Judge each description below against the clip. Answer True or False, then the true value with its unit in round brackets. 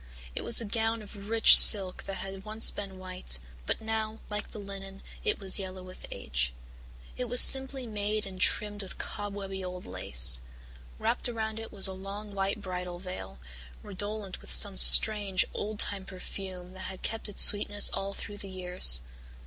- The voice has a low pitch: False (200 Hz)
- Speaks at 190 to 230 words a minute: False (175 wpm)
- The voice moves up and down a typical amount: False (2.3 semitones)